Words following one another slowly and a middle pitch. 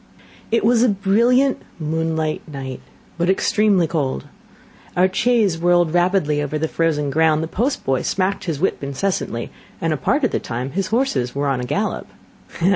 No: average, 170 wpm; medium, 165 Hz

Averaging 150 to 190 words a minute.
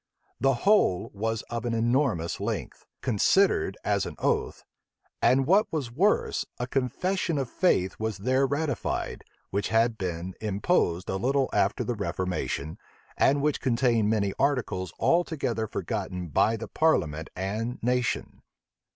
No: slow, 135 wpm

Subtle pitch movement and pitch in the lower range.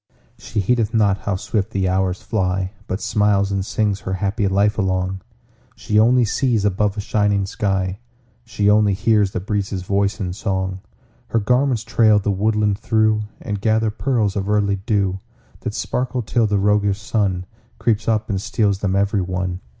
Yes: narrow, 2.1 semitones; low, 100 Hz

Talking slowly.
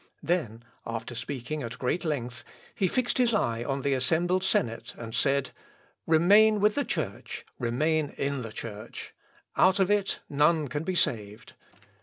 No: average, 155 wpm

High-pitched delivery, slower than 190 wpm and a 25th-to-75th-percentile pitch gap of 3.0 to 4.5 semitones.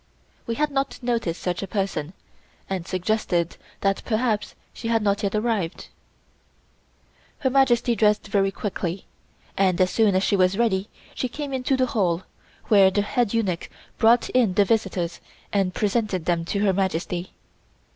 Yes: high, 200 Hz; average, 155 wpm; average, 3.7 semitones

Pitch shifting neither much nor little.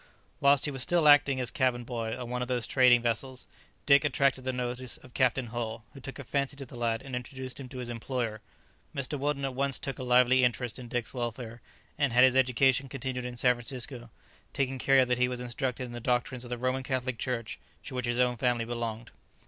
No: narrow, 1.6 semitones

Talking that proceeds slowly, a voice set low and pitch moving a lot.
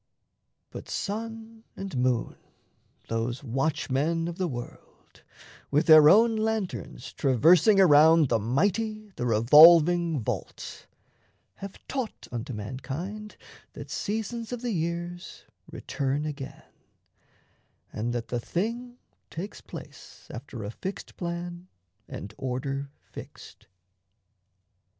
No: slow, 105 wpm; medium, 165 Hz; wide, 7.5 semitones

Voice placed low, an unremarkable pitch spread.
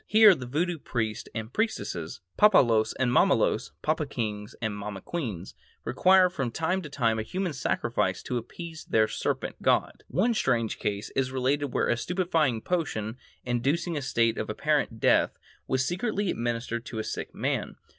No: low, 130 Hz; wide, 7.3 semitones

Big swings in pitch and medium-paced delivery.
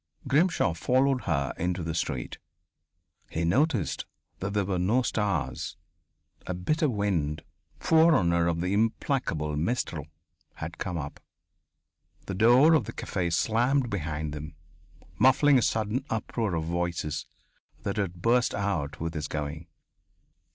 No: wide, 6.9 semitones; slow, 130 wpm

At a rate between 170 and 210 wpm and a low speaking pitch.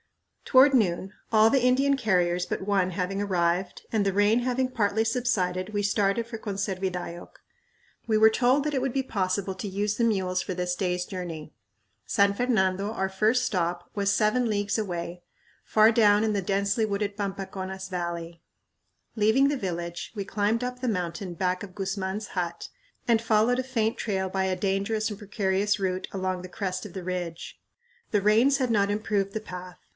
No: average, 180 wpm; high, 200 Hz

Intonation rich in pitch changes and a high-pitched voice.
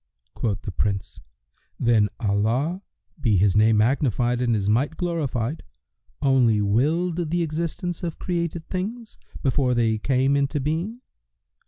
No: wide, 7.0 semitones; low, 135 Hz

